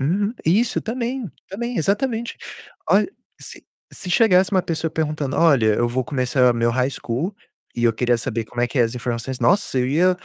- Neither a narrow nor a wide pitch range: No, wide, 8.2 semitones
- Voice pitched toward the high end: No, medium, 150 Hz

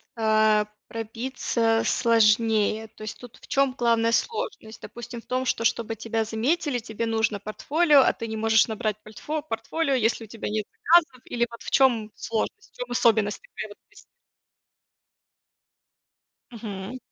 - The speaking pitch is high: Yes, high, 230 Hz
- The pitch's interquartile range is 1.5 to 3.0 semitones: Yes, narrow, 2.5 semitones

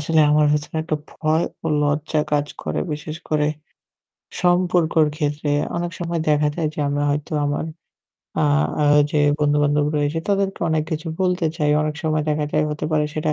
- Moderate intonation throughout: No, narrow, 1.6 semitones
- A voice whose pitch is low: No, medium, 155 Hz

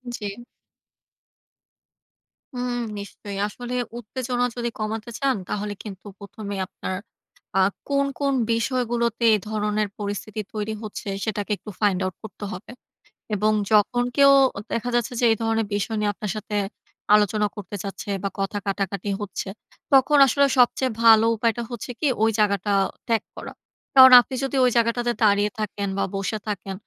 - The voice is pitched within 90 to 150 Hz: No, high, 215 Hz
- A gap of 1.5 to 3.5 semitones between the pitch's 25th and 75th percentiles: Yes, average, 2.8 semitones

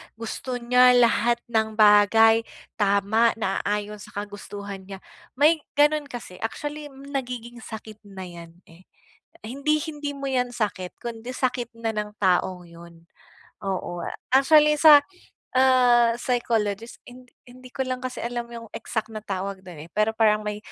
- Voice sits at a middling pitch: No, high, 230 Hz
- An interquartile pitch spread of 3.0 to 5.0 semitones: Yes, average, 3.8 semitones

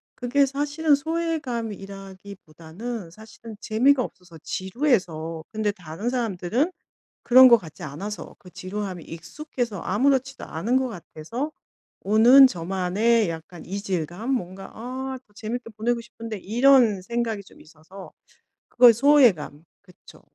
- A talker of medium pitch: No, high, 220 Hz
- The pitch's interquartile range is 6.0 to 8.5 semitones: No, wide, 5.4 semitones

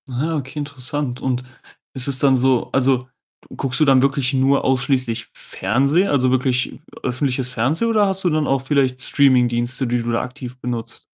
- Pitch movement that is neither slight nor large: No, narrow, 2.1 semitones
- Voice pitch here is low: Yes, low, 130 Hz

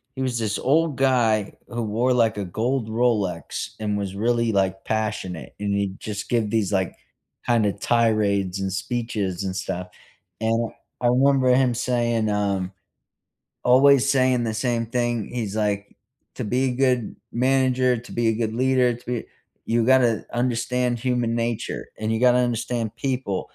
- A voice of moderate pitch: No, low, 115 Hz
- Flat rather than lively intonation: No, average, 3.0 semitones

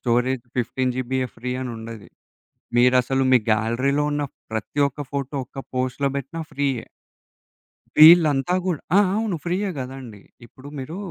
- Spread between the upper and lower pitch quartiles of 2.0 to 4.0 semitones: Yes, average, 2.9 semitones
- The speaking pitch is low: Yes, low, 130 Hz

